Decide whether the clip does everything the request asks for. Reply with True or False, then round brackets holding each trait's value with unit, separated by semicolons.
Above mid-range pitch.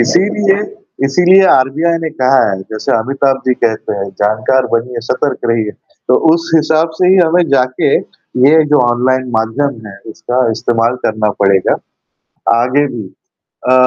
False (130 Hz)